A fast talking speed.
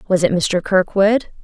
No: average, 165 wpm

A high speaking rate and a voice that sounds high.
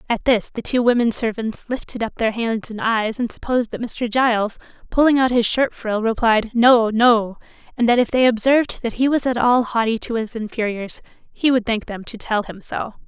Yes: fast, 215 wpm; high, 230 Hz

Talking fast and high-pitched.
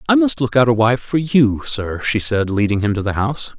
No: fast, 270 wpm; low, 115 Hz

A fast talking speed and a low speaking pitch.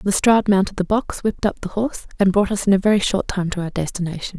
No: fast, 260 wpm; high, 195 Hz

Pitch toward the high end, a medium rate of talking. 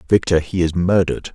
No: very low, 85 Hz; average, 180 wpm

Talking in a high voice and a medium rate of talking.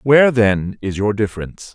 No: low, 110 Hz; average, 170 wpm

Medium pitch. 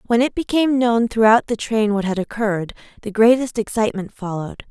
No: high, 220 Hz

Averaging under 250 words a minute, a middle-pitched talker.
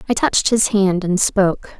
No: average, 200 wpm; high, 200 Hz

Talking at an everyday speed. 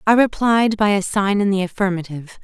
Yes: average, 195 wpm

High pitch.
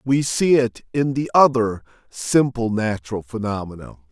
No: low, 125 Hz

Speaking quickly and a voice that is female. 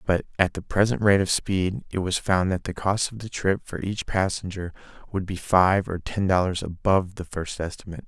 No: fast, 215 wpm; male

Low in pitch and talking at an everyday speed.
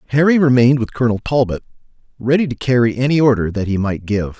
Yes: low, 125 Hz; average, 190 wpm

